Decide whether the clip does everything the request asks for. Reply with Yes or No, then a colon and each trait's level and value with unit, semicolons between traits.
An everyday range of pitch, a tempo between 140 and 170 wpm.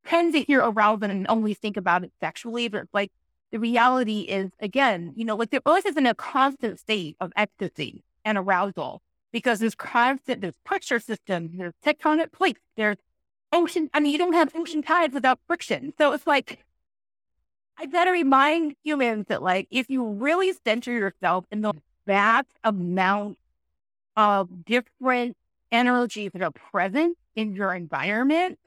No: wide, 6.5 semitones; average, 160 wpm